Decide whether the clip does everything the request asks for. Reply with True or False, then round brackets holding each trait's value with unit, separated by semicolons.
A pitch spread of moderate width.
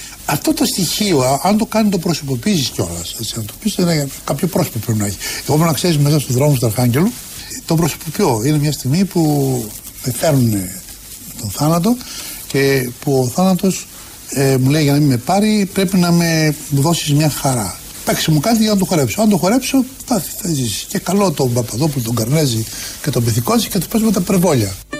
False (7.0 semitones)